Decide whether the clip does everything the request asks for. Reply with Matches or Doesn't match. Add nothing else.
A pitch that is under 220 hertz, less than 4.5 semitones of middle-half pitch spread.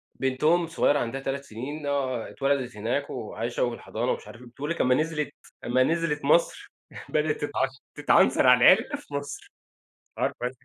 Matches